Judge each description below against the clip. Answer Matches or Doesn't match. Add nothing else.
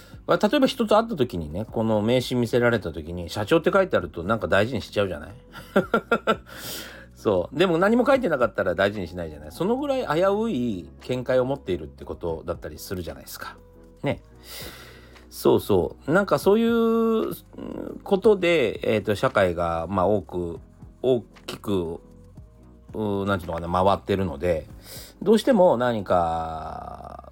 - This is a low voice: Matches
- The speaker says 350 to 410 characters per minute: Doesn't match